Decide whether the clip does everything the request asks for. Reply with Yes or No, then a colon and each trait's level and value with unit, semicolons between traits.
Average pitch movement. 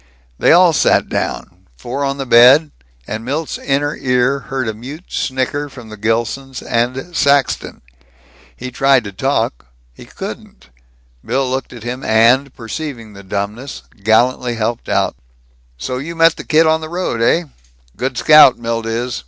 Yes: average, 3.5 semitones